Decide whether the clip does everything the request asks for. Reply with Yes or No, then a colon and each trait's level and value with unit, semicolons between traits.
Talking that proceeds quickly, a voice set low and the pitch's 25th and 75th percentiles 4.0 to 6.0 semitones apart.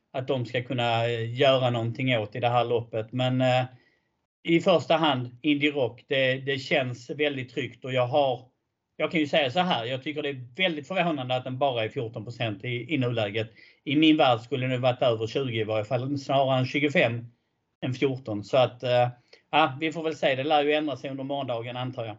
No: fast, 210 wpm; low, 130 Hz; average, 3.5 semitones